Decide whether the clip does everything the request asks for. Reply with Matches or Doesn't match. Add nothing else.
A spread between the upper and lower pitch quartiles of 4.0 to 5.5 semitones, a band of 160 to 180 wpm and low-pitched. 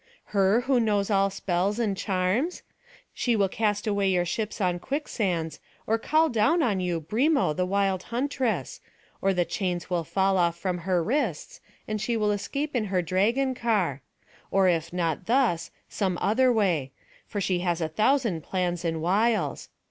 Doesn't match